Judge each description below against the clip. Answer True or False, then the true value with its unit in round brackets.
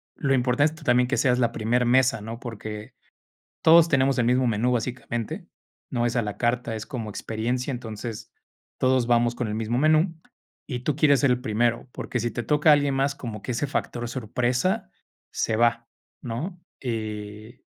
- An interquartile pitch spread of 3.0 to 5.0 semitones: False (2.5 semitones)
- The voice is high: False (120 Hz)